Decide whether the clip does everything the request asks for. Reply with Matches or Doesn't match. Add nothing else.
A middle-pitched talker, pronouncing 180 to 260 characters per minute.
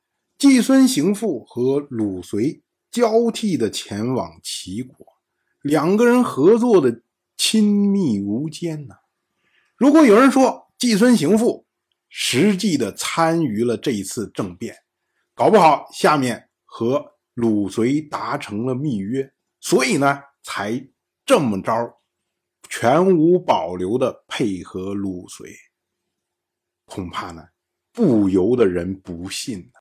Doesn't match